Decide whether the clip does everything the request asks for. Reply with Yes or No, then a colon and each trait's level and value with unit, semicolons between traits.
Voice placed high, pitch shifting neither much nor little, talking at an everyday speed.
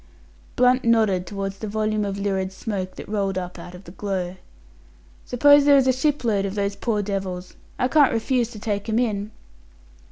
Yes: high, 205 Hz; average, 3.4 semitones; average, 185 wpm